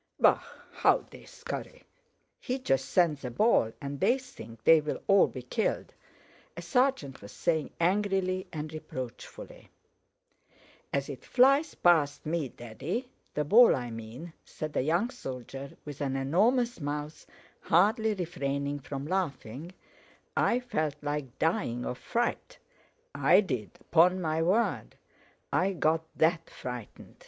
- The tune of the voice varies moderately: No, wide, 6.2 semitones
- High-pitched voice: No, medium, 160 Hz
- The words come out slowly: Yes, slow, 130 wpm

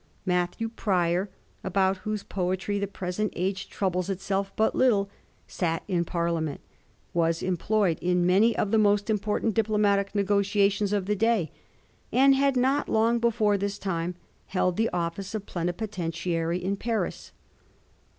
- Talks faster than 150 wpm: No, average, 145 wpm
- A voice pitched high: Yes, high, 200 Hz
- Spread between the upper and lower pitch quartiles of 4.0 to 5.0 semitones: No, average, 3.0 semitones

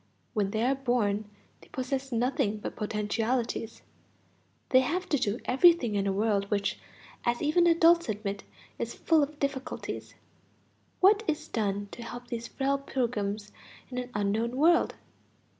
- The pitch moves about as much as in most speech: Yes, average, 4.8 semitones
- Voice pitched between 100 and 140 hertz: No, high, 240 Hz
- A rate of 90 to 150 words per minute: Yes, average, 145 wpm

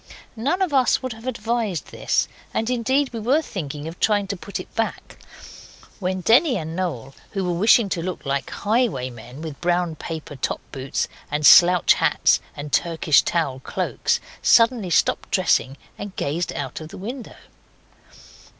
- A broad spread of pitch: Yes, wide, 6.7 semitones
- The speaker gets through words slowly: No, average, 160 wpm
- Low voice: No, medium, 180 Hz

